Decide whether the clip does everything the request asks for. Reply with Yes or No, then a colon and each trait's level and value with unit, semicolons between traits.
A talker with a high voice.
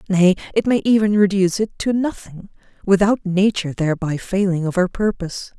Yes: high, 195 Hz